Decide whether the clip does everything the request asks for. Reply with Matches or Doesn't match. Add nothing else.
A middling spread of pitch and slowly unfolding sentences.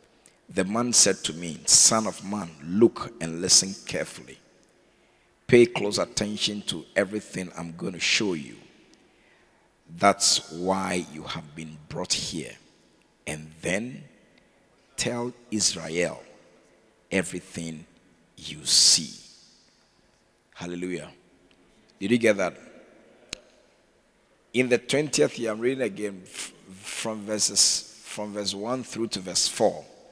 Matches